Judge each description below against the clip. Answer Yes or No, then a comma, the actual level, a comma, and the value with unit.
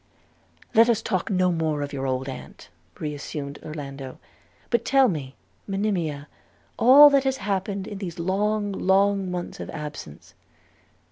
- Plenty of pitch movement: Yes, wide, 6.0 semitones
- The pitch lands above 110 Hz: Yes, medium, 185 Hz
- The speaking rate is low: No, average, 145 wpm